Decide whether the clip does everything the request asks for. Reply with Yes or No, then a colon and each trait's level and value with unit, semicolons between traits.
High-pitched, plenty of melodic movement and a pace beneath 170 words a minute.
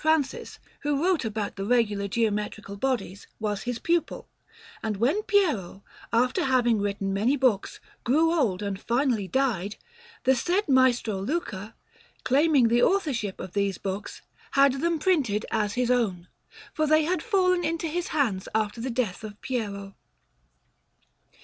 Yes: high, 240 Hz; wide, 6.3 semitones; average, 145 wpm